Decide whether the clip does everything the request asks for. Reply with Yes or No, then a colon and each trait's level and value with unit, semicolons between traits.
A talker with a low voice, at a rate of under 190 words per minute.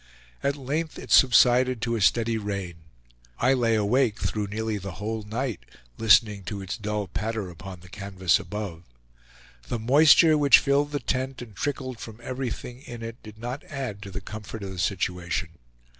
Yes: low, 110 Hz; average, 175 wpm